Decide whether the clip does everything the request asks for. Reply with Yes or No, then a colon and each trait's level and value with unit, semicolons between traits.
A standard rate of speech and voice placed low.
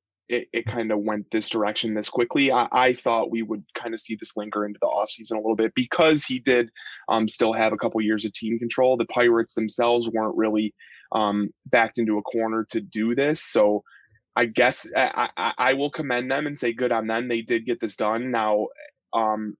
No: fast, 215 wpm; low, 115 Hz